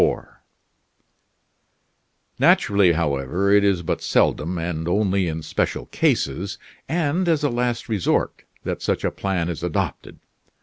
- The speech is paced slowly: Yes, slow, 125 wpm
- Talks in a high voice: No, very low, 95 Hz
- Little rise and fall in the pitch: No, average, 4.4 semitones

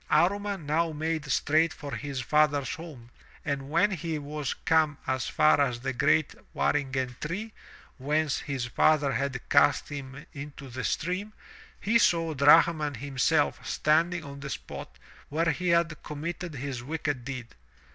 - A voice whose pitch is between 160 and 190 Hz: No, medium, 150 Hz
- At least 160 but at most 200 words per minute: No, average, 145 wpm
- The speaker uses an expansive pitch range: No, average, 3.0 semitones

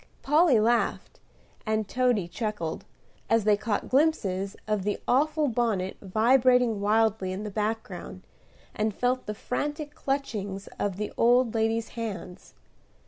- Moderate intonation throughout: Yes, average, 3.6 semitones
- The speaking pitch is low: No, high, 220 Hz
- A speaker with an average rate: No, slow, 130 wpm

